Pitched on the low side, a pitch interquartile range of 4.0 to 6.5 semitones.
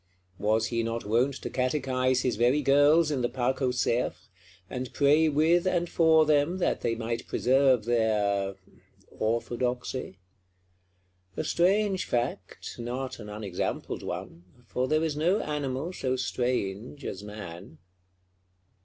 Yes: low, 125 Hz; average, 4.5 semitones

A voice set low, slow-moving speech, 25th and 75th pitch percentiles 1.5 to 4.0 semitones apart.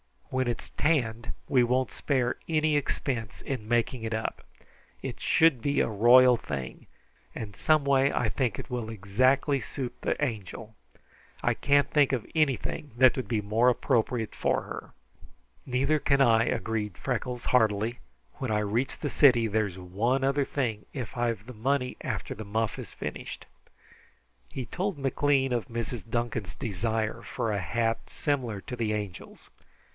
No: low, 120 Hz; average, 160 wpm; average, 3.5 semitones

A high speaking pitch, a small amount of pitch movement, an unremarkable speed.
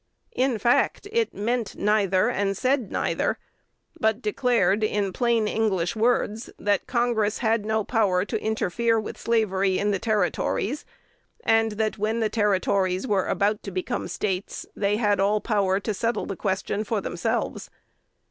Yes: high, 210 Hz; narrow, 2.3 semitones; average, 150 wpm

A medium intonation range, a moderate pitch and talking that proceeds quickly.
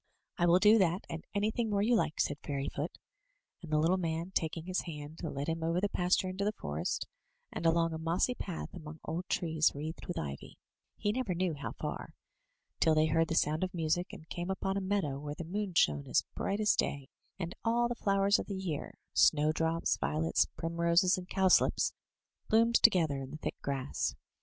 Yes: average, 3.5 semitones; medium, 170 Hz; fast, 210 wpm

